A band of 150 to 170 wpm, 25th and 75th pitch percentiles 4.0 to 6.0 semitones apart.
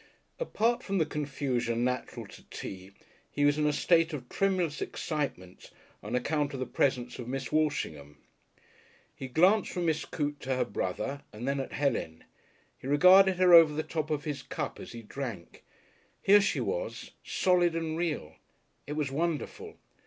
Yes: average, 165 wpm; average, 4.8 semitones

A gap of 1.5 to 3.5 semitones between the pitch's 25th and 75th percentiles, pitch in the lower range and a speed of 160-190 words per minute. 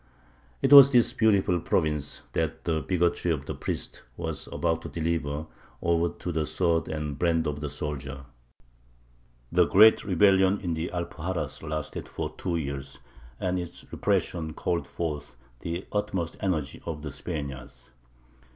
No: average, 3.1 semitones; very low, 80 Hz; average, 150 wpm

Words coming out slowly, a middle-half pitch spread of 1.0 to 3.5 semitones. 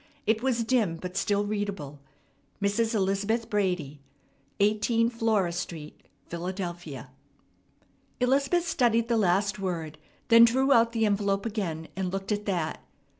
No: slow, 125 wpm; average, 4.2 semitones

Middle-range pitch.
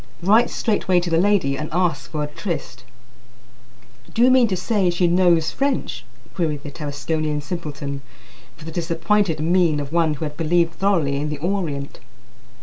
Yes: medium, 165 Hz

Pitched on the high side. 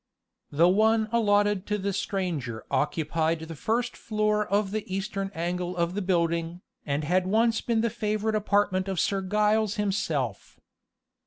Yes: high, 195 Hz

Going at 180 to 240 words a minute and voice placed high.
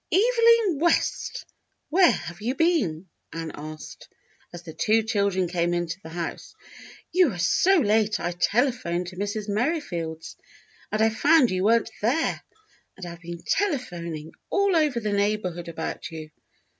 No: average, 145 wpm; high, 205 Hz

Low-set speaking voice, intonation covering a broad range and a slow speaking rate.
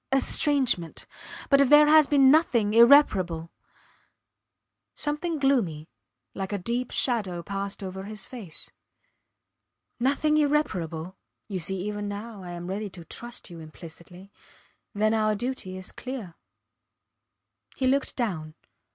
No: high, 210 Hz; wide, 6.5 semitones; slow, 125 wpm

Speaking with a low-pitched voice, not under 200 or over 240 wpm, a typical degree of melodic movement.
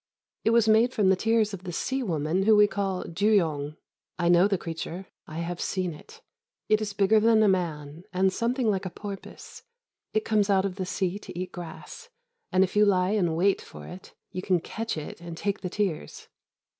No: high, 190 Hz; fast, 205 wpm; average, 3.3 semitones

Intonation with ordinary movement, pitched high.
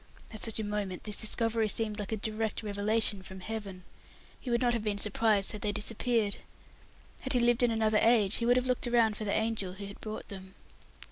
No: narrow, 1.9 semitones; high, 215 Hz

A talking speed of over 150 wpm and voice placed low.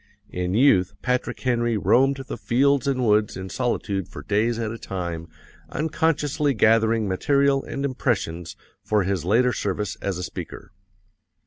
No: average, 145 wpm; low, 115 Hz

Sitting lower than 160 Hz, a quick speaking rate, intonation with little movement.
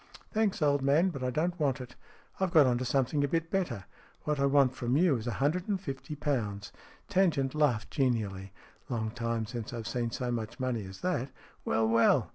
No: low, 135 Hz; fast, 210 wpm; average, 4.7 semitones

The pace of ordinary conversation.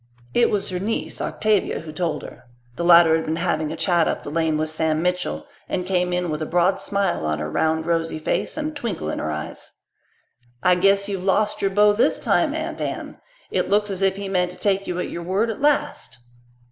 No: fast, 225 wpm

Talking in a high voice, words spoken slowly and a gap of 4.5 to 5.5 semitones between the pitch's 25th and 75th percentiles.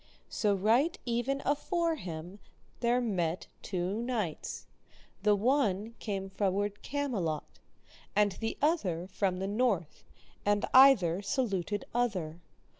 Yes: high, 205 Hz; slow, 115 wpm; average, 4.8 semitones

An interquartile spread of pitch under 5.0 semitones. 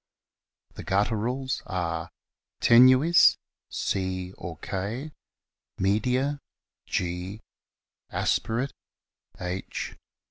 No: wide, 5.6 semitones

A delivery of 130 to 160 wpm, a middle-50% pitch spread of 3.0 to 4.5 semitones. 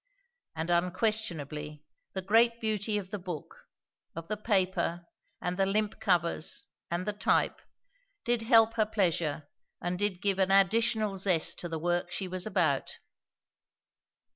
Yes: average, 140 wpm; average, 3.6 semitones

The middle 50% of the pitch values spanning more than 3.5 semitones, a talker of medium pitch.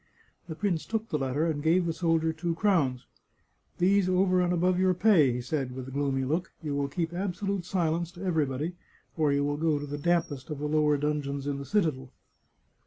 Yes: average, 3.9 semitones; medium, 160 Hz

